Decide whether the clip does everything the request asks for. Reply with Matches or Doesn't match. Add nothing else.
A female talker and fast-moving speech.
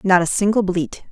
Matches